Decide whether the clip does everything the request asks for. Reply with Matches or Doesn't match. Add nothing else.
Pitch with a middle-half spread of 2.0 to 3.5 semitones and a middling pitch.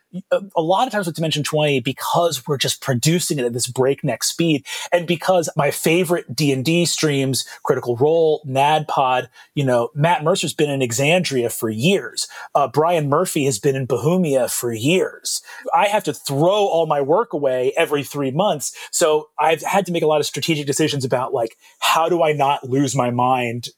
Doesn't match